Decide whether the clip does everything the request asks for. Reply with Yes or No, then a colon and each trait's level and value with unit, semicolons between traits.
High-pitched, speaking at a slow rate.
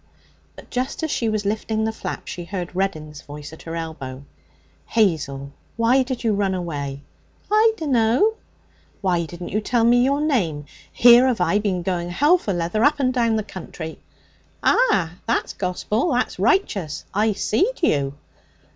No: high, 205 Hz; average, 165 wpm